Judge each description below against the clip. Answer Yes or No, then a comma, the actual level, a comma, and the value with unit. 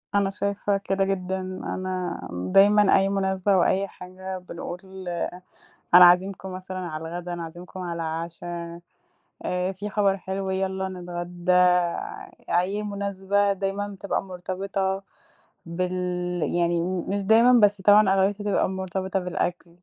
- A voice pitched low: No, high, 190 Hz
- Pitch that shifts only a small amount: Yes, narrow, 1.7 semitones